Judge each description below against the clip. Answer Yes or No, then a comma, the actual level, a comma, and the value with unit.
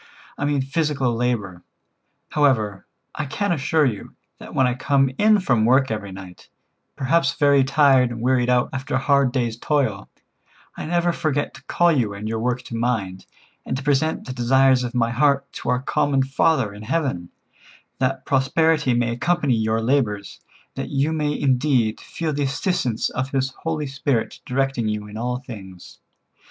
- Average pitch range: Yes, average, 3.4 semitones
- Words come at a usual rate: Yes, average, 175 wpm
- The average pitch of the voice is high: No, low, 130 Hz